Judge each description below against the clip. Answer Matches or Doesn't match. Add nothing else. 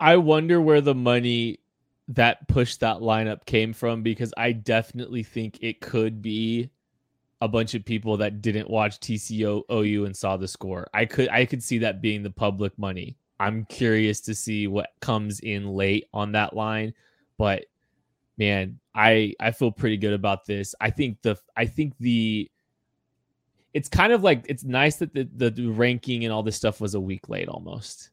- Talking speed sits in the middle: Matches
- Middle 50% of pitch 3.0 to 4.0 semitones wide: Doesn't match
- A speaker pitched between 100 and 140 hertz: Matches